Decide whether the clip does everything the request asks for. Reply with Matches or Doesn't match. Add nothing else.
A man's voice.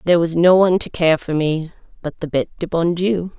Doesn't match